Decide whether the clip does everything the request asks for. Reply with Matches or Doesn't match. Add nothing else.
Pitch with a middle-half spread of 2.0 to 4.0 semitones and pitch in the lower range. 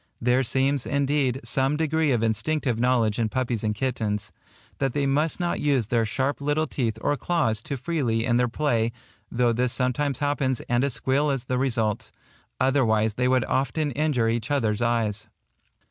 Matches